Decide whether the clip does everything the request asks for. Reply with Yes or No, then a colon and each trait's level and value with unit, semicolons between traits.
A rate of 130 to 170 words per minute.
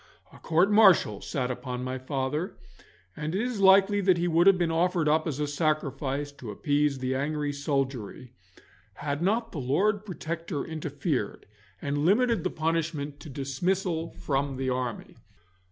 Yes: average, 155 wpm